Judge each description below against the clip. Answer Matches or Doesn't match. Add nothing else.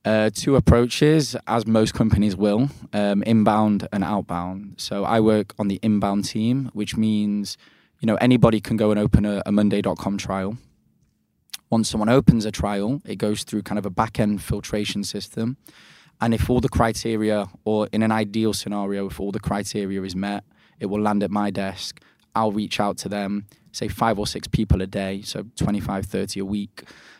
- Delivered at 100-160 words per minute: Doesn't match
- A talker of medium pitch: Doesn't match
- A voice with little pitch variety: Matches